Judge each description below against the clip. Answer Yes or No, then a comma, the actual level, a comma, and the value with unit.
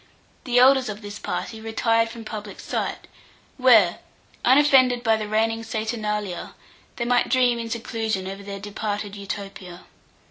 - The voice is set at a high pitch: Yes, high, 220 Hz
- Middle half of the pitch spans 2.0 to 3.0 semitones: Yes, narrow, 2.6 semitones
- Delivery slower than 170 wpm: Yes, average, 140 wpm